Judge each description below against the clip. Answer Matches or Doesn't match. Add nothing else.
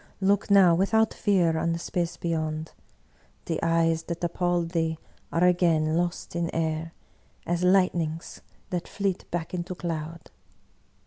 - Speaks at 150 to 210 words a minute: Doesn't match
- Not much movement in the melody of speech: Matches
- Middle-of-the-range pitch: Matches